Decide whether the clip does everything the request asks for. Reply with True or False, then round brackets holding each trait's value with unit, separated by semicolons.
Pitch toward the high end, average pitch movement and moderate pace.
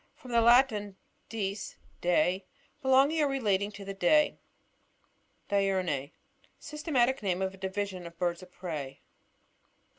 True (200 Hz; 5.0 semitones; 145 wpm)